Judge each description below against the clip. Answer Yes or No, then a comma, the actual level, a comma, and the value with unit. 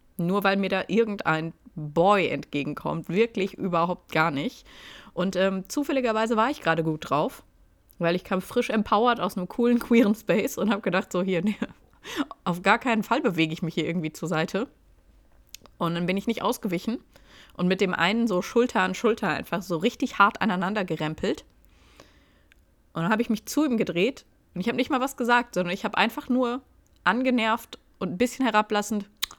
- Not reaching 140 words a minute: No, average, 185 wpm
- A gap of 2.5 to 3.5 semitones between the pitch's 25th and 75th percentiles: No, average, 4.9 semitones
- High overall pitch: Yes, high, 200 Hz